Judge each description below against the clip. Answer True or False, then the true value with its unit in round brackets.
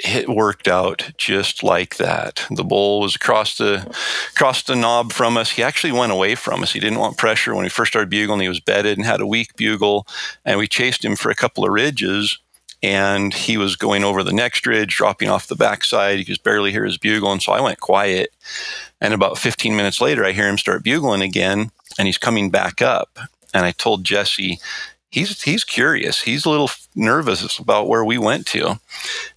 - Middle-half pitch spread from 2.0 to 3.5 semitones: True (2.8 semitones)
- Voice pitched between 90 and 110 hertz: True (105 Hz)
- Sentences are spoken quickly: True (210 wpm)